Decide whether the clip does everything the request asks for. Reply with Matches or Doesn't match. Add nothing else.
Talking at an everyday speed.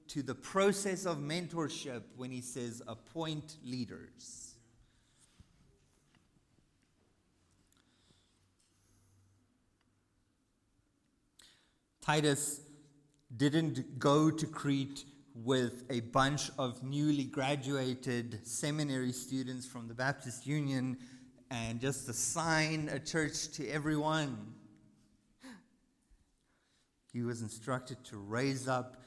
Doesn't match